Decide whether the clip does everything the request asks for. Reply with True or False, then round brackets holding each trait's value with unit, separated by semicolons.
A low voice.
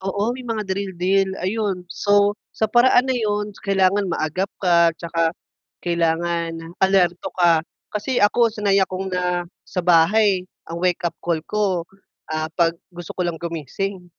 False (185 Hz)